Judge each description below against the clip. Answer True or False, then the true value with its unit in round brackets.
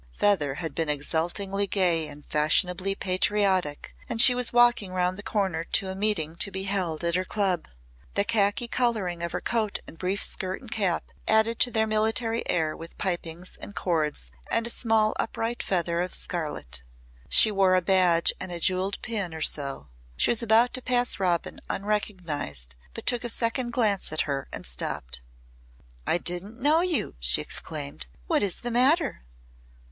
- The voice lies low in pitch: False (190 Hz)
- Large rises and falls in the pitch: False (4.8 semitones)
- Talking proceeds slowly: False (175 wpm)